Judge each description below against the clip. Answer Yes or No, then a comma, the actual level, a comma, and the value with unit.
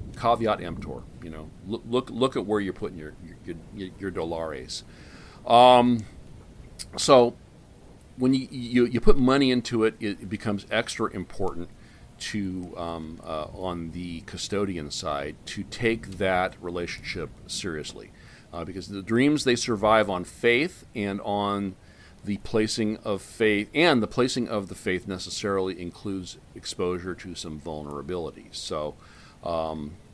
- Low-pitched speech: Yes, low, 100 Hz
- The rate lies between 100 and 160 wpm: Yes, average, 140 wpm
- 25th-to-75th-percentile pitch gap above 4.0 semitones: Yes, average, 4.4 semitones